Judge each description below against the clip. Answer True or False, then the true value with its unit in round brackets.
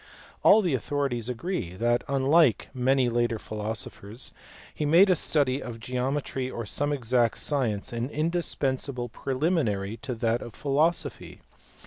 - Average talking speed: False (130 wpm)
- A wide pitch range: False (3.8 semitones)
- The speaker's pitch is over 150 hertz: False (130 Hz)